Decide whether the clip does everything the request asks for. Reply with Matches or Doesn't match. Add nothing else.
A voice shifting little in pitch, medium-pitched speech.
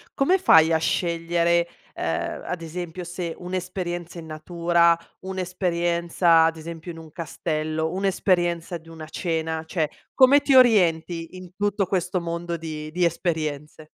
Matches